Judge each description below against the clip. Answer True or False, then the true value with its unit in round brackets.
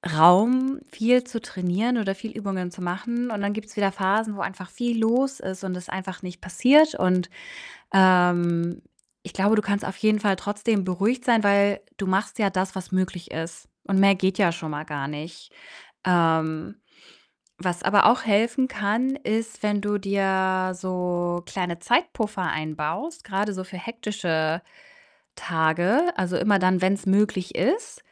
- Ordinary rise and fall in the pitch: True (3.3 semitones)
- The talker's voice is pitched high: True (195 Hz)